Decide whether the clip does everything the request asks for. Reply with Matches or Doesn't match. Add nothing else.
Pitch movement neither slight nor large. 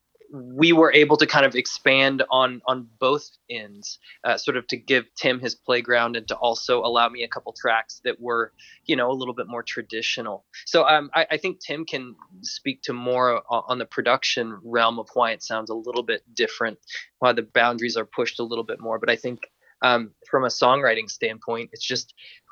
Matches